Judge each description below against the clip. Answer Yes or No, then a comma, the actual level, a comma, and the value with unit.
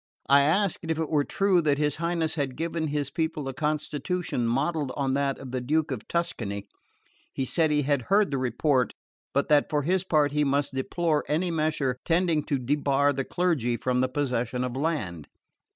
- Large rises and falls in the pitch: No, average, 3.4 semitones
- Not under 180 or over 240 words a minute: Yes, average, 190 wpm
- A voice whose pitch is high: No, medium, 145 Hz